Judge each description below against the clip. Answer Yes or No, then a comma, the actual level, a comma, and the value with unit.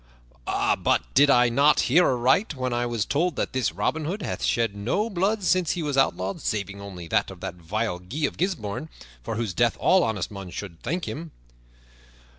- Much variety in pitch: Yes, wide, 7.9 semitones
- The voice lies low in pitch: Yes, low, 125 Hz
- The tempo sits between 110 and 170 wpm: No, average, 195 wpm